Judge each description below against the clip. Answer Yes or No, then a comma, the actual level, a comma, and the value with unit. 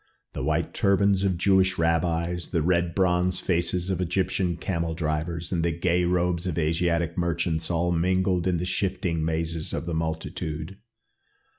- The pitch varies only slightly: Yes, narrow, 1.8 semitones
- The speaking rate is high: No, average, 155 wpm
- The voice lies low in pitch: Yes, very low, 85 Hz